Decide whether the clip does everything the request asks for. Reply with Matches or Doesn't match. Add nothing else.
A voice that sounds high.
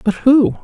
Matches